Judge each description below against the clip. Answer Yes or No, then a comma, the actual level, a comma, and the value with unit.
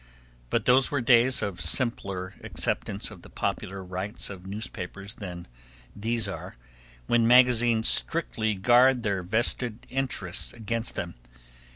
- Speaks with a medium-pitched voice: No, low, 110 Hz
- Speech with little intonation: No, average, 3.8 semitones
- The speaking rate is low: Yes, slow, 130 wpm